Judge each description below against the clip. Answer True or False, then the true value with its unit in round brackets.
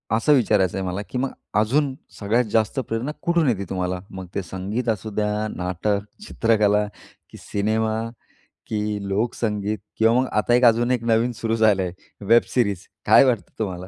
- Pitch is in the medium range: False (110 Hz)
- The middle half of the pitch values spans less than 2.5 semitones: False (2.8 semitones)